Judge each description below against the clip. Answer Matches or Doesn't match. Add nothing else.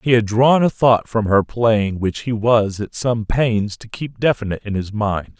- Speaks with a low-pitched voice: Matches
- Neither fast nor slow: Doesn't match